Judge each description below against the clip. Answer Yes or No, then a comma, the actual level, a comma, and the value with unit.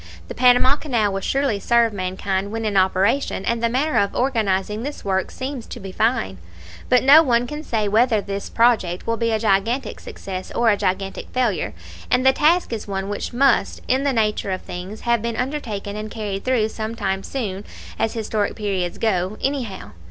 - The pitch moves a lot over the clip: No, average, 4.0 semitones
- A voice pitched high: Yes, high, 220 Hz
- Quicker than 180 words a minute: Yes, average, 190 wpm